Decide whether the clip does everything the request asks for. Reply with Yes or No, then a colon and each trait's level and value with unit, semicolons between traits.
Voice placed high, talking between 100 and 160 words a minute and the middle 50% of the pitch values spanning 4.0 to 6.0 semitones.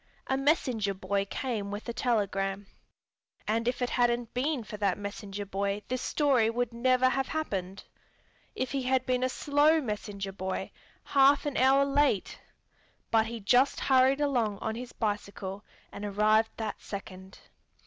Yes: high, 230 Hz; average, 150 wpm; average, 4.4 semitones